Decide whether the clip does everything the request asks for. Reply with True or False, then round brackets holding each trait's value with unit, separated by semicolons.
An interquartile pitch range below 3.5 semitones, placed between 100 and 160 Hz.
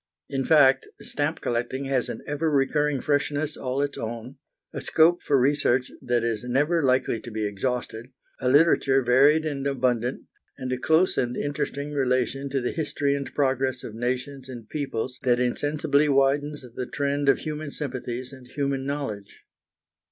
True (2.5 semitones; 135 Hz)